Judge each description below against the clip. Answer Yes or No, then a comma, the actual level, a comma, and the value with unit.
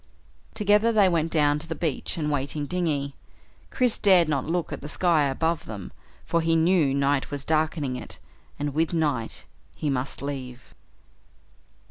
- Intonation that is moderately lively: Yes, average, 3.2 semitones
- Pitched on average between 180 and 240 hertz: No, medium, 155 Hz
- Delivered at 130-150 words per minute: No, average, 170 wpm